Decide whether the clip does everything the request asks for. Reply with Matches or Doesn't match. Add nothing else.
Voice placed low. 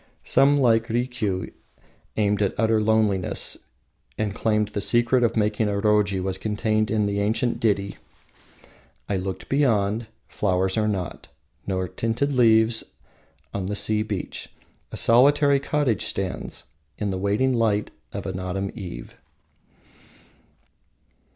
Matches